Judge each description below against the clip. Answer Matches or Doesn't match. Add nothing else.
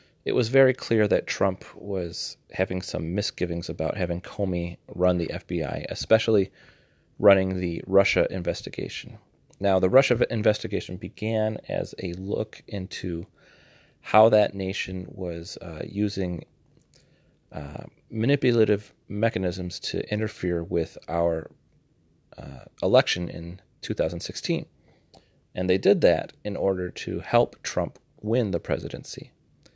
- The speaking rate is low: Matches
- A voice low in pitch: Matches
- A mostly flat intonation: Doesn't match